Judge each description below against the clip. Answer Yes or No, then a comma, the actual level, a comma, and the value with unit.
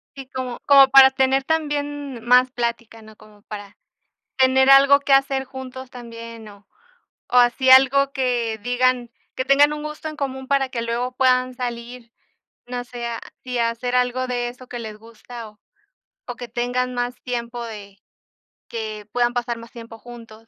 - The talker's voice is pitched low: No, high, 245 Hz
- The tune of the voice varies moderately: No, narrow, 2.1 semitones